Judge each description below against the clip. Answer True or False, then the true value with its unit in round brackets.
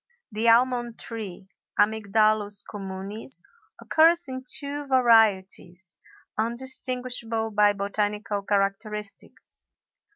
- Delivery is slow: True (75 wpm)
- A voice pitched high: True (215 Hz)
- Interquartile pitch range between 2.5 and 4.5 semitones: True (3.3 semitones)